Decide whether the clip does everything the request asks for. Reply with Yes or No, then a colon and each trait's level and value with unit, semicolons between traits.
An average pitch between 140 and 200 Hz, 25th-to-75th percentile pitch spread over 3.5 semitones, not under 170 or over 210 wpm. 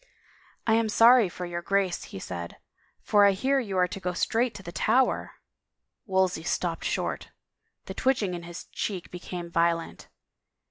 Yes: medium, 185 Hz; average, 4.1 semitones; average, 190 wpm